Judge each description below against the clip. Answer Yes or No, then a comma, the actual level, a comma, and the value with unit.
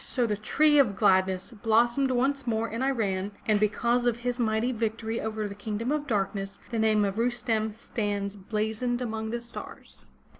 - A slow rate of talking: No, average, 175 wpm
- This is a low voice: No, high, 220 Hz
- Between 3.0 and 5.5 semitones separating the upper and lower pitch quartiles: No, narrow, 2.5 semitones